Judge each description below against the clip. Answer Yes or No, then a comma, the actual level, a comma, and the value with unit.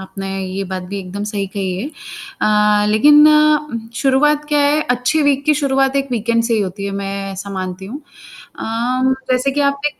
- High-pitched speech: Yes, high, 235 Hz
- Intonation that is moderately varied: No, wide, 6.0 semitones